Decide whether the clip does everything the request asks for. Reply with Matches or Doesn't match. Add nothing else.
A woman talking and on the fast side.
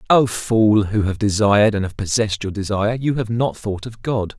Doesn't match